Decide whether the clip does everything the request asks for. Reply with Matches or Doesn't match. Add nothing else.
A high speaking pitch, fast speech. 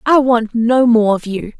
Matches